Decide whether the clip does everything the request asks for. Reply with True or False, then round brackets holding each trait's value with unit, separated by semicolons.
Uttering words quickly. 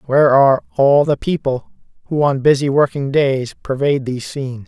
False (165 wpm)